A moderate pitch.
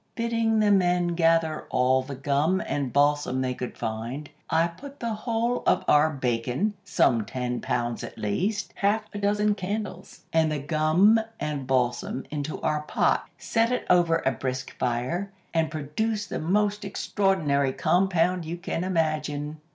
Yes: medium, 160 Hz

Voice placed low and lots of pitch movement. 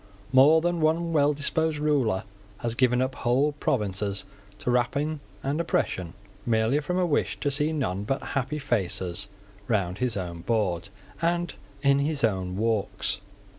Yes: low, 130 Hz; wide, 6.4 semitones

